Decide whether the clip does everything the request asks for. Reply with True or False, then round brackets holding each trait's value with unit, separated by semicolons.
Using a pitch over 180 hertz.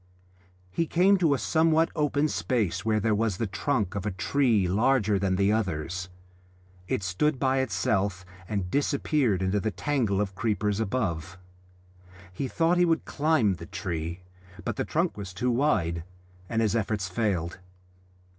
False (105 Hz)